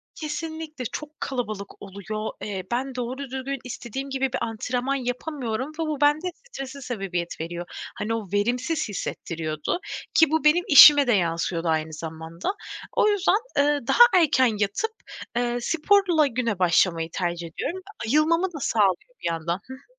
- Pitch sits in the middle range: No, very high, 250 Hz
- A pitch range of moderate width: No, wide, 7.5 semitones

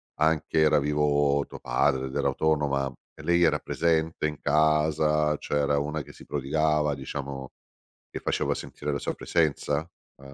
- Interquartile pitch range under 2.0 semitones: Yes, narrow, 1.6 semitones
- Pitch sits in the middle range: No, very low, 75 Hz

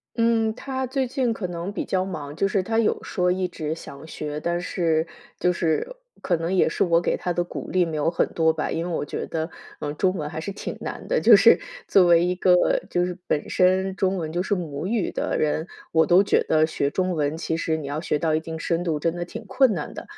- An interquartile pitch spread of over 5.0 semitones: No, average, 3.0 semitones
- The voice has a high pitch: No, medium, 175 Hz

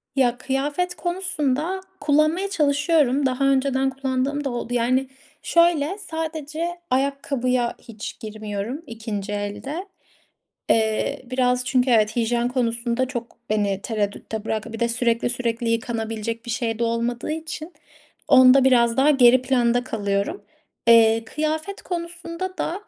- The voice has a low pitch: No, very high, 255 Hz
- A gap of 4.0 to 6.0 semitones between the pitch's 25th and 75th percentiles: Yes, average, 4.3 semitones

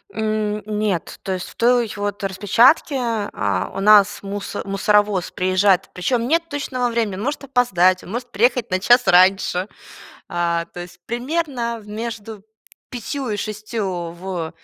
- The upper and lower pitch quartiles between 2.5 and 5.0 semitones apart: Yes, average, 4.2 semitones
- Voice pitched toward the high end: Yes, high, 210 Hz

